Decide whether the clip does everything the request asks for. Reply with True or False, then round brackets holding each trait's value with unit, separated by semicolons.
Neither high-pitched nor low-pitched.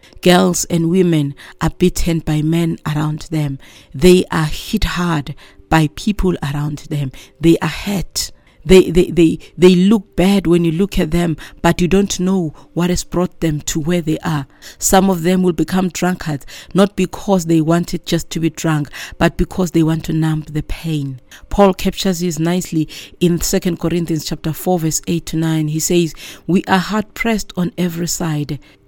True (170 Hz)